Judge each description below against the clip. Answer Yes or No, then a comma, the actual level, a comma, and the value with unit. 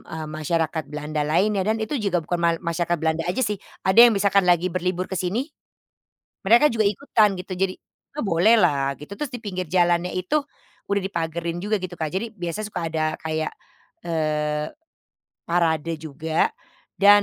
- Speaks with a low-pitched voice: No, medium, 175 Hz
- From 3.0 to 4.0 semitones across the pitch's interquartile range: Yes, average, 3.7 semitones